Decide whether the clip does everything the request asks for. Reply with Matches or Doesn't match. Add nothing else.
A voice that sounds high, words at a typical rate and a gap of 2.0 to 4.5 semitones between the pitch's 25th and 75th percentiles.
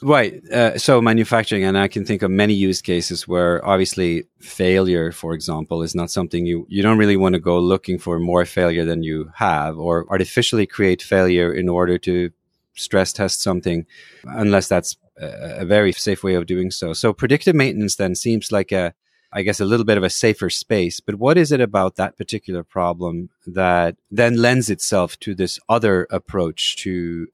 Doesn't match